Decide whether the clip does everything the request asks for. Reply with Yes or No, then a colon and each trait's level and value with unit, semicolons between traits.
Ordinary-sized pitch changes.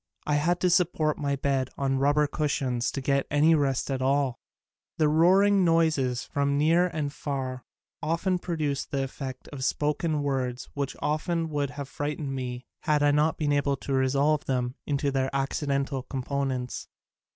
No: narrow, 2.3 semitones